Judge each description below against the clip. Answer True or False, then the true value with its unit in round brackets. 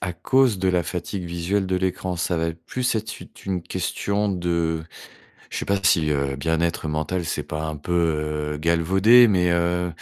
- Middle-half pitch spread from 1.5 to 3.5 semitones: True (2.6 semitones)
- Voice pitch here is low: True (90 Hz)